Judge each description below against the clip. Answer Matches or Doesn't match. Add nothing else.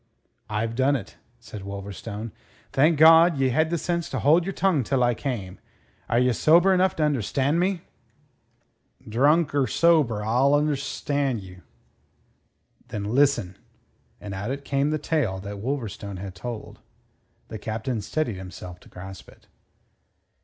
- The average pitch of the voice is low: Matches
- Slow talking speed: Doesn't match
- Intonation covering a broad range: Matches